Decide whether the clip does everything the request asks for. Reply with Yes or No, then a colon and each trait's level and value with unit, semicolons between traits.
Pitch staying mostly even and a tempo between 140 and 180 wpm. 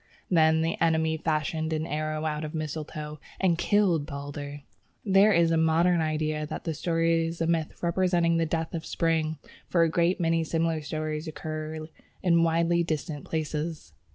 Yes: narrow, 1.3 semitones; average, 170 wpm